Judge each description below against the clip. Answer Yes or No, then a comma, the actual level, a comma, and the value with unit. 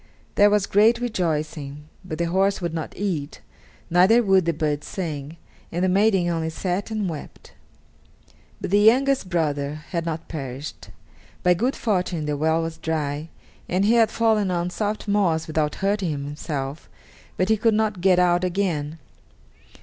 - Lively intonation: No, average, 4.5 semitones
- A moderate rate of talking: Yes, average, 160 wpm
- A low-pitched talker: No, medium, 175 Hz